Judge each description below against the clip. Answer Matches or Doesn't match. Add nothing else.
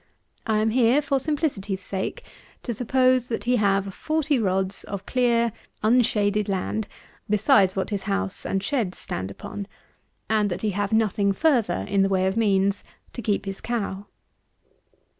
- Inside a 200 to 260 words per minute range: Doesn't match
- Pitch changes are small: Doesn't match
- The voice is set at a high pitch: Matches